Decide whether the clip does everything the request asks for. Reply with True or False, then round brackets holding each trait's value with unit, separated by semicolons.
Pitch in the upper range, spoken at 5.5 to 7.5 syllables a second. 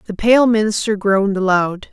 False (205 Hz; 5.1 syllables/s)